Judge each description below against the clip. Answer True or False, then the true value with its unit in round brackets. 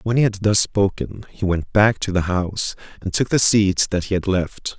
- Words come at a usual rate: False (240 wpm)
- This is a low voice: True (100 Hz)